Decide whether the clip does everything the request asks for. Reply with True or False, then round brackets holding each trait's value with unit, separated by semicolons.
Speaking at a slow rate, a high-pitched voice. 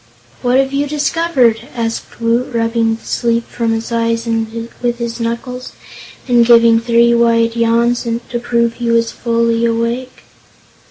False (145 wpm; 235 Hz)